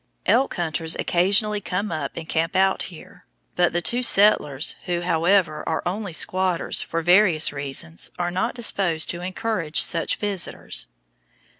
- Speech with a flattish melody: No, average, 3.3 semitones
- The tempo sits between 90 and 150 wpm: Yes, average, 145 wpm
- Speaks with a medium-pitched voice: Yes, medium, 175 Hz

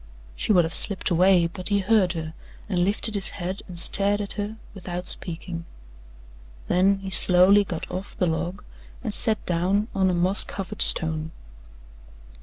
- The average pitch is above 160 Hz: Yes, medium, 185 Hz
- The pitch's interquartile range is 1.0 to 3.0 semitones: Yes, narrow, 2.6 semitones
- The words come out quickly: No, average, 165 wpm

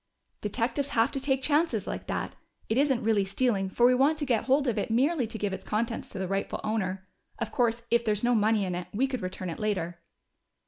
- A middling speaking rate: No, fast, 230 wpm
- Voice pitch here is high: Yes, high, 225 Hz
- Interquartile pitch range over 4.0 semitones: Yes, average, 4.5 semitones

